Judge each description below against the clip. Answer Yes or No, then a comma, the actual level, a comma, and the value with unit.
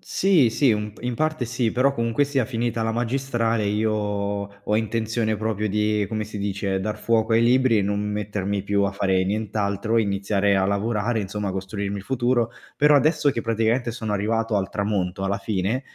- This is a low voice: Yes, low, 110 Hz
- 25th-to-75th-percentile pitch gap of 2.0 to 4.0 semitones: Yes, narrow, 2.5 semitones